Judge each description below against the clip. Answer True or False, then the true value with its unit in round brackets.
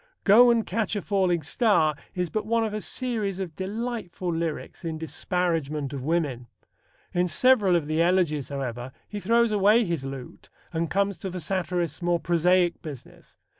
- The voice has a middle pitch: True (180 Hz)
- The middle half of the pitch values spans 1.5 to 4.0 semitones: False (4.5 semitones)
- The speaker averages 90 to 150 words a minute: False (170 wpm)